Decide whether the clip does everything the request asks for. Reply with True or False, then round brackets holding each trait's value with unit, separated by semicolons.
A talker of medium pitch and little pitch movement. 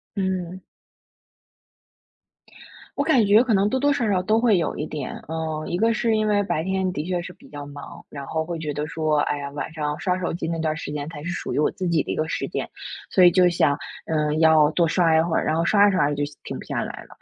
False (165 Hz; 3.7 semitones)